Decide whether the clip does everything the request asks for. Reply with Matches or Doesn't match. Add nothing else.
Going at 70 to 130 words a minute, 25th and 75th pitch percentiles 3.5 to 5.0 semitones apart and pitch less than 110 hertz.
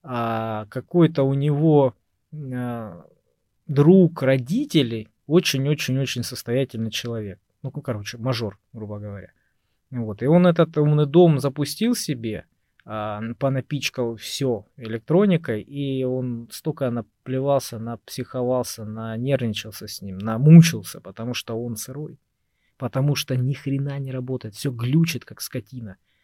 Doesn't match